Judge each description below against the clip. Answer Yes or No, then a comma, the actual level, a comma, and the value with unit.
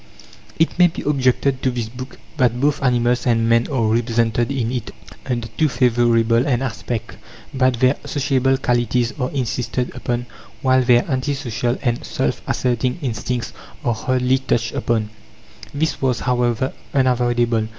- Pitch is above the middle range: No, low, 125 Hz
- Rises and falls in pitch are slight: Yes, narrow, 1.8 semitones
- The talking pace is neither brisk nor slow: Yes, average, 150 wpm